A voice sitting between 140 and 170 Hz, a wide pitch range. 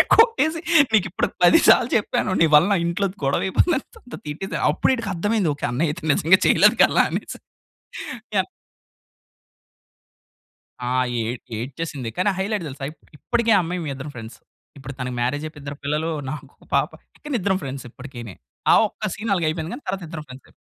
Yes: medium, 165 Hz; wide, 6.3 semitones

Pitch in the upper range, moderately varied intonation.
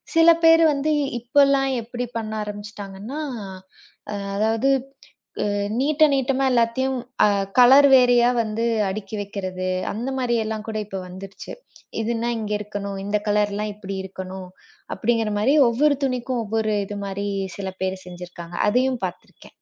Yes: high, 220 Hz; average, 4.1 semitones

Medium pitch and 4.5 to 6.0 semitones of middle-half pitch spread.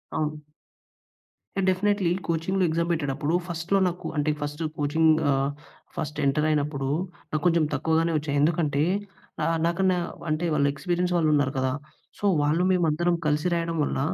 No: medium, 160 Hz; average, 2.7 semitones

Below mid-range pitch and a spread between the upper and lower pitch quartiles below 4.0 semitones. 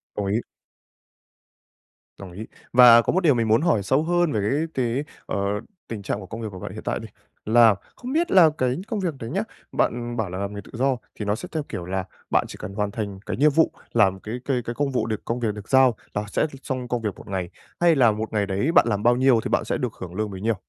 No: low, 115 Hz; average, 4.4 semitones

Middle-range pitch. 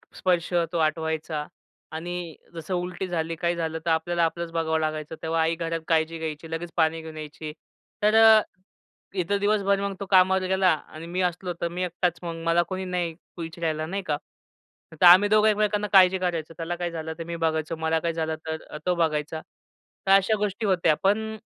Yes: medium, 170 Hz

